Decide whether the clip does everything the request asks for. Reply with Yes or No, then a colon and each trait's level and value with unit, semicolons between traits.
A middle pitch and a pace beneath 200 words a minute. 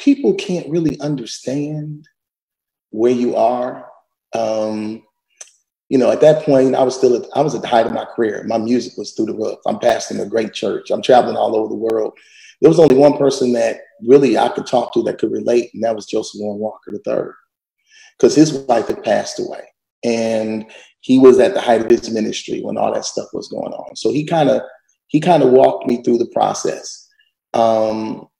No: medium, 145 Hz; fast, 205 wpm